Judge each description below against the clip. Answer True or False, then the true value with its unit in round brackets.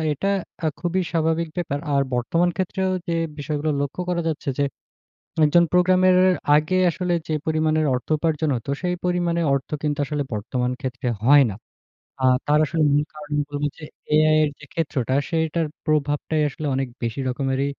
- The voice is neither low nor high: True (155 Hz)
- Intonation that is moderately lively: True (3.0 semitones)